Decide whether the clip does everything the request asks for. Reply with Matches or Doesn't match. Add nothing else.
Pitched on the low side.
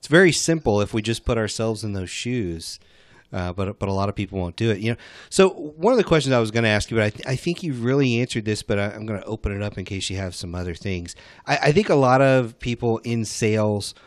Matches